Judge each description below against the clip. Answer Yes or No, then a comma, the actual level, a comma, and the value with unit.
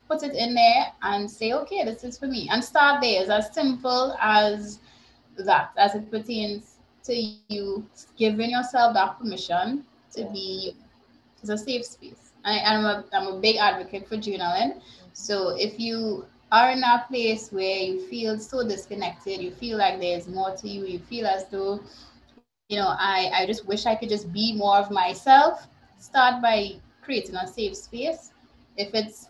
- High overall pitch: Yes, high, 215 Hz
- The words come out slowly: No, average, 180 wpm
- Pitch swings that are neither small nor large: Yes, average, 3.4 semitones